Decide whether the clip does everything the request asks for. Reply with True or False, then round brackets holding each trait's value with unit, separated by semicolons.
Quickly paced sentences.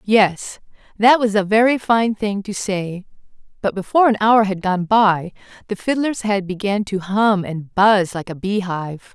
False (175 wpm)